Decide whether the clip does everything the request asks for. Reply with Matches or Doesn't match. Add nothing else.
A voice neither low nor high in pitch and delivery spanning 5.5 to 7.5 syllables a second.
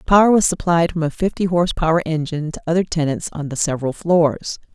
Matches